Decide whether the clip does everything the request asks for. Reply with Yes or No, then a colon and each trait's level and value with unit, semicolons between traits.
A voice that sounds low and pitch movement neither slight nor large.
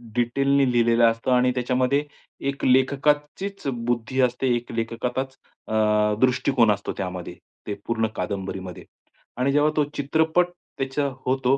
Yes: low, 125 Hz; average, 3.1 semitones